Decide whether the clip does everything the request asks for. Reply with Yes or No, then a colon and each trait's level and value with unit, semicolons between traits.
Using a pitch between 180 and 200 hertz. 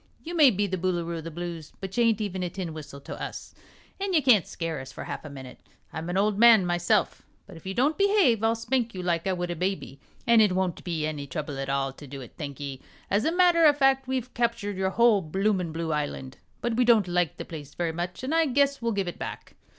Yes: high, 190 Hz